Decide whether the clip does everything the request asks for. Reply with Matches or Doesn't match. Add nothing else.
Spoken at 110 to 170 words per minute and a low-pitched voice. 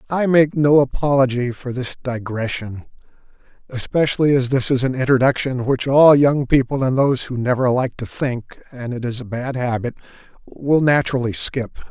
Matches